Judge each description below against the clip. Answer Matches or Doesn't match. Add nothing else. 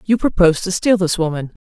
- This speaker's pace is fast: Matches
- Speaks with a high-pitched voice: Doesn't match